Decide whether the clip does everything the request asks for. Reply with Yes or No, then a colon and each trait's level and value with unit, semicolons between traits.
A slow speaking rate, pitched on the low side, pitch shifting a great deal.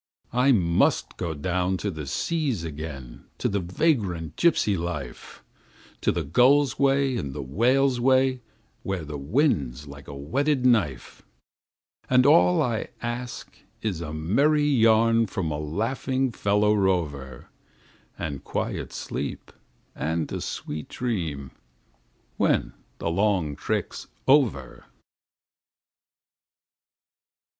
Yes: slow, 115 wpm; very low, 95 Hz; wide, 8.6 semitones